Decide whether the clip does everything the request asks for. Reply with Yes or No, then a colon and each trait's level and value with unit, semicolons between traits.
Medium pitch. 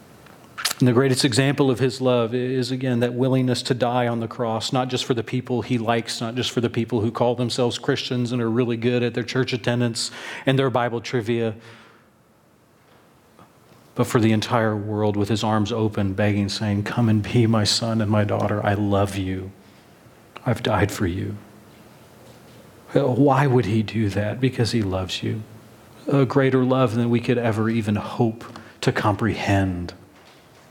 No: low, 115 Hz